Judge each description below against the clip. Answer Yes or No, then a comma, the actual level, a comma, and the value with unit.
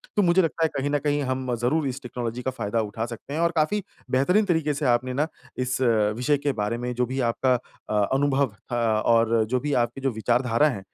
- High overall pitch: No, low, 130 Hz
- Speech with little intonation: No, average, 3.6 semitones